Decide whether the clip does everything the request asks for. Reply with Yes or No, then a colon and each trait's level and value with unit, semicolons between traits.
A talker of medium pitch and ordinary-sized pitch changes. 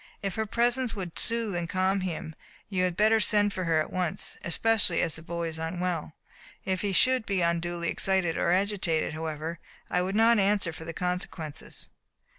Yes: medium, 180 Hz; average, 3.5 semitones